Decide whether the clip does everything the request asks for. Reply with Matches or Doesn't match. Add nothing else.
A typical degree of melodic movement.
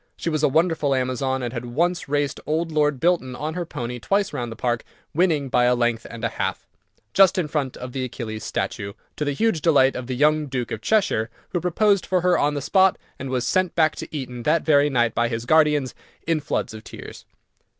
Matches